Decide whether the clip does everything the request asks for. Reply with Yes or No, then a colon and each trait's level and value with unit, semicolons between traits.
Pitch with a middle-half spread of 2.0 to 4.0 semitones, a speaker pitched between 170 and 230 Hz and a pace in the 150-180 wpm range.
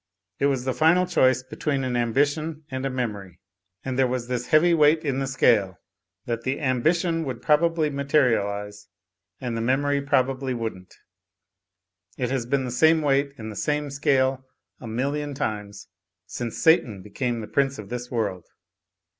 No: average, 3.5 semitones; low, 130 Hz; average, 165 wpm